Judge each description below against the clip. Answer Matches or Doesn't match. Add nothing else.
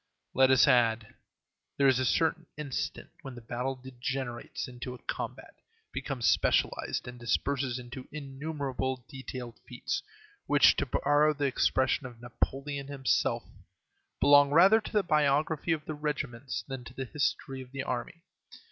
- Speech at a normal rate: Matches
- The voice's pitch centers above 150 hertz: Doesn't match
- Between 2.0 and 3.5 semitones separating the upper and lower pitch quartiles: Matches